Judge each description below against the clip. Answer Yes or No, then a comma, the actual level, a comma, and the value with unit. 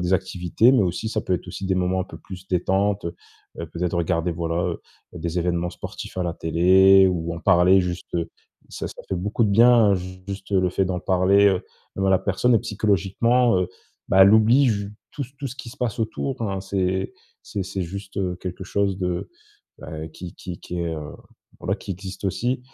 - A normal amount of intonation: No, narrow, 2.2 semitones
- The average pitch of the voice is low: Yes, very low, 95 Hz